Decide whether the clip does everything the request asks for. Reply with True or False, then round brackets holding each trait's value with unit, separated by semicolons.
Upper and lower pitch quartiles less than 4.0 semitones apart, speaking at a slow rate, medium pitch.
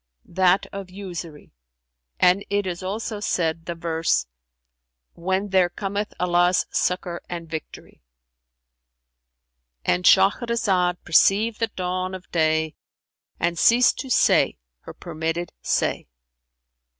True (3.3 semitones; 105 wpm; 175 Hz)